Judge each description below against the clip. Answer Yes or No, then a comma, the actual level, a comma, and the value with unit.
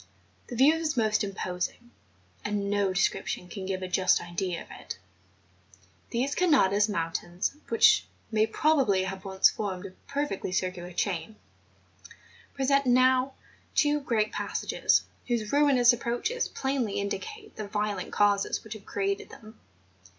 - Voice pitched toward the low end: No, high, 215 Hz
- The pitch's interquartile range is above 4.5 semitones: Yes, average, 5.2 semitones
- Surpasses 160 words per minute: No, slow, 135 wpm